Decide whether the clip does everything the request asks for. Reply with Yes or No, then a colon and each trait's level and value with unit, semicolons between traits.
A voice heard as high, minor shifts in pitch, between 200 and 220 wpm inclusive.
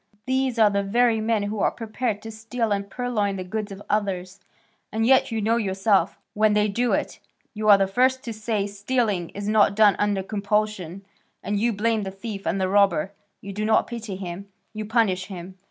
Yes: high, 210 Hz; narrow, 2.2 semitones; fast, 205 wpm